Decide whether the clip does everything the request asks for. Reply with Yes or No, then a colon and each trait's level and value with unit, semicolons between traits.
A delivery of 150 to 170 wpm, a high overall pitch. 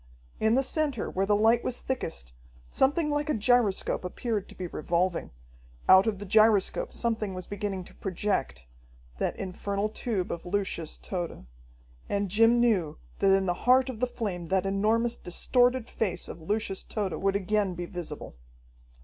Yes: average, 165 wpm; high, 205 Hz